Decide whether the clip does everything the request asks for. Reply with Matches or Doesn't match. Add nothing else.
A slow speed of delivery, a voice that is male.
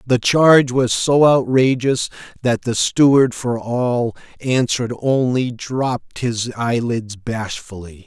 Matches